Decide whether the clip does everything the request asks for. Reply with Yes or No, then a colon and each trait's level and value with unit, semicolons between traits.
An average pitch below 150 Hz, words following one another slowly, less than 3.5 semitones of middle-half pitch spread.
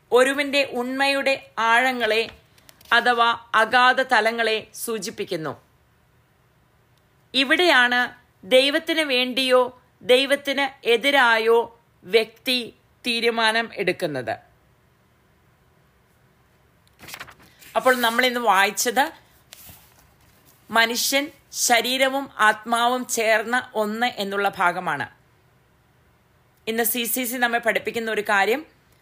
No: high, 235 Hz; slow, 70 wpm; average, 2.9 semitones